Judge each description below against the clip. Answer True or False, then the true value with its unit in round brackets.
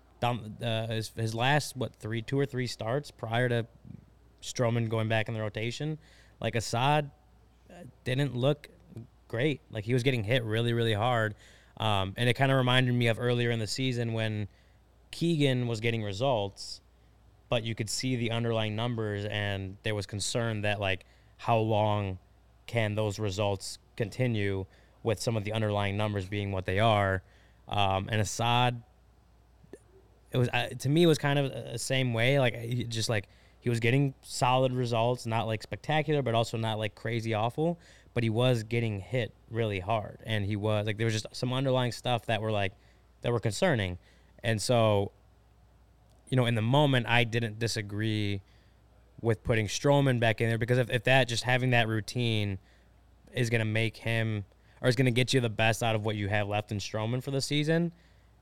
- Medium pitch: False (115 Hz)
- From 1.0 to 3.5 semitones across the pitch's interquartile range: True (3.0 semitones)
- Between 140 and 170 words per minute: False (185 wpm)